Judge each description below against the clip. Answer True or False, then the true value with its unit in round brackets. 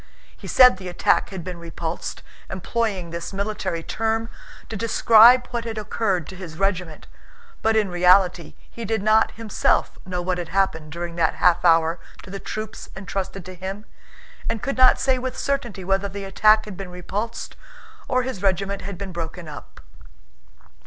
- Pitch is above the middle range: True (195 Hz)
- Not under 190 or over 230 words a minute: False (170 wpm)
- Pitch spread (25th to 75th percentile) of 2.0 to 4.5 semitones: True (3.7 semitones)